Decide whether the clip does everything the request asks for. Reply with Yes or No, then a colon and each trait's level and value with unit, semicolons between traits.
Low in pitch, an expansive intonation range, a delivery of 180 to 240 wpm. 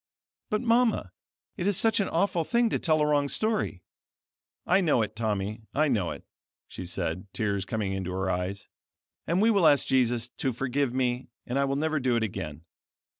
Yes: low, 130 Hz; wide, 8.8 semitones; average, 190 wpm